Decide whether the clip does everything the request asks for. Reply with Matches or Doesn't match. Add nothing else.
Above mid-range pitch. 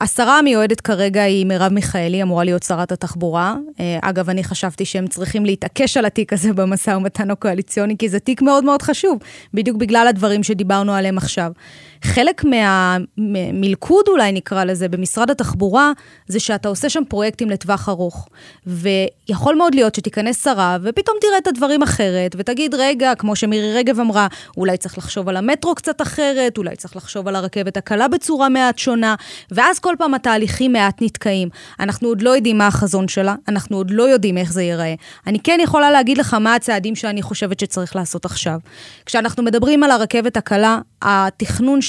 Matches